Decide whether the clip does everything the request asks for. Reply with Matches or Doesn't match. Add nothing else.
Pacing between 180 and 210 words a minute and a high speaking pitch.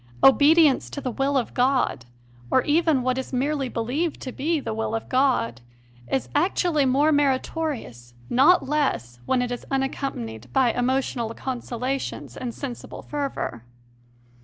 Doesn't match